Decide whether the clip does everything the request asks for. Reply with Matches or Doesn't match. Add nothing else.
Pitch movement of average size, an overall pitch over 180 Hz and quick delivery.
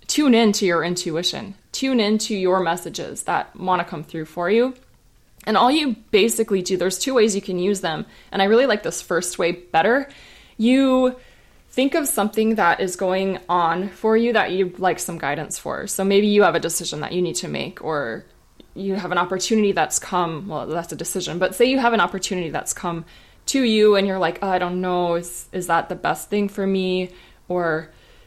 Matches